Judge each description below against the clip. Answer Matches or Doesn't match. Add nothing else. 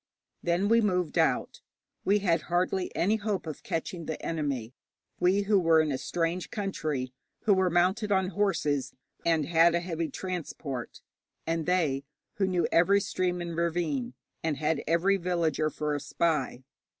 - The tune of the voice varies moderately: Matches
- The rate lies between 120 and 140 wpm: Doesn't match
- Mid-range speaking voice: Matches